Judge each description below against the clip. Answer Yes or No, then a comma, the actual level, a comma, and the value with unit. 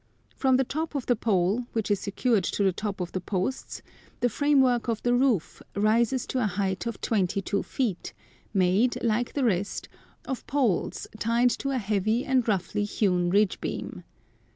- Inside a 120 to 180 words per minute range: Yes, average, 175 wpm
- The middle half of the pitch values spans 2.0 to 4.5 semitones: Yes, average, 4.1 semitones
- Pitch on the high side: Yes, high, 220 Hz